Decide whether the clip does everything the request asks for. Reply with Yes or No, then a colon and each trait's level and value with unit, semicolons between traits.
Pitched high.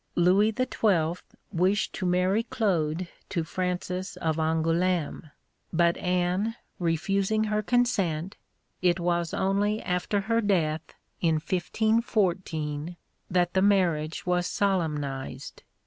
No: medium, 180 Hz